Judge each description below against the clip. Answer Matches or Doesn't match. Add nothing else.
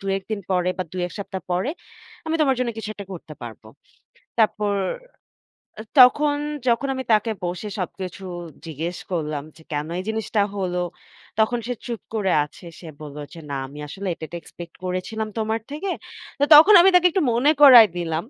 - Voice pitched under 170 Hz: Doesn't match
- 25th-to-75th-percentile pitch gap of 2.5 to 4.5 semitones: Doesn't match